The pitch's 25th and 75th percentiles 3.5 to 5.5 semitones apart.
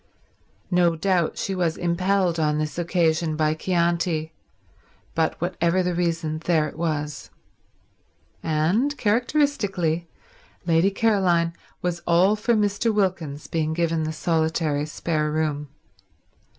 No: average, 2.8 semitones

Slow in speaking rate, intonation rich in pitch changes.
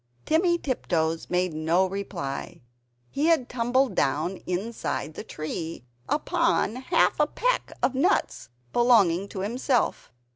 Yes: slow, 120 wpm; wide, 8.4 semitones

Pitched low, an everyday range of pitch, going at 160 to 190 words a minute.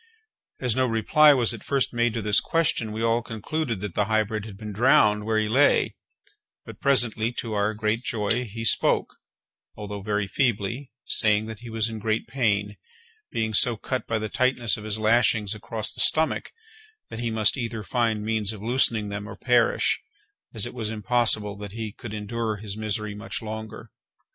No: low, 110 Hz; narrow, 2.0 semitones; average, 185 wpm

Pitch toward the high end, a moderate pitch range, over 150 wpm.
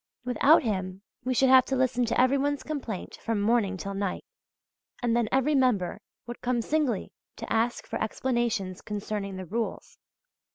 Yes: high, 235 Hz; average, 4.3 semitones; average, 165 wpm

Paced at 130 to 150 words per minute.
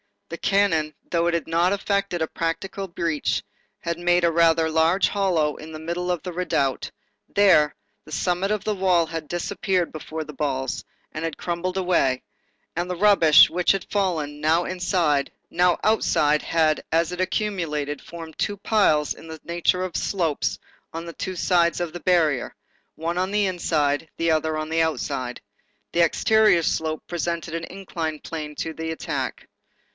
No: average, 170 wpm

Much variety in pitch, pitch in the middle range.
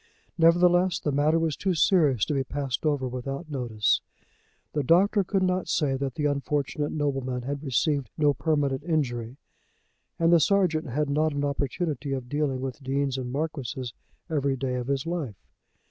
No: average, 3.0 semitones; medium, 145 Hz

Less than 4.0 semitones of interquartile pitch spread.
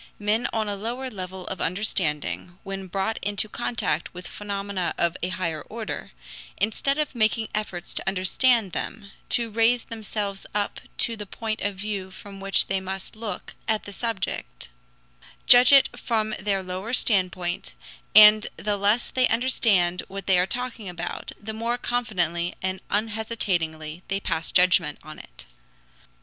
Yes: average, 3.3 semitones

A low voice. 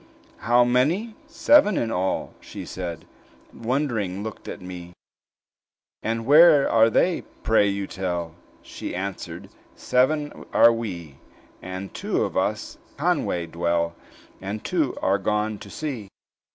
Yes: low, 110 Hz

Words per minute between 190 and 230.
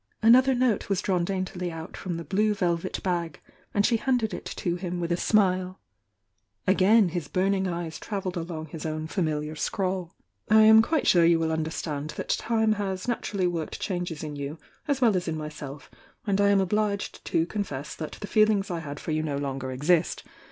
Yes: average, 195 wpm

